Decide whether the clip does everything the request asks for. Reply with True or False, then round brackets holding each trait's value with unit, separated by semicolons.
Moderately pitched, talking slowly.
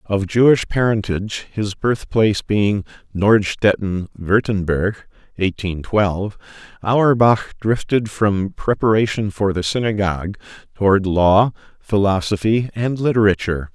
False (100 Hz; 95 wpm)